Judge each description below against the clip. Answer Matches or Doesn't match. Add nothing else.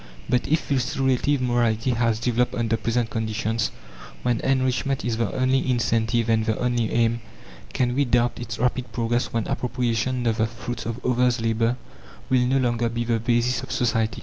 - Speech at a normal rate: Matches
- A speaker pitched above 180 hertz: Doesn't match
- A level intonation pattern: Matches